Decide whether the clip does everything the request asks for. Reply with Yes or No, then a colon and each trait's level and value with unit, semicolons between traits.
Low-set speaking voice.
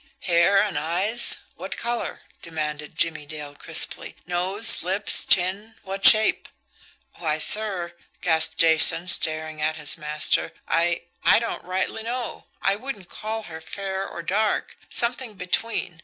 No: medium, 180 Hz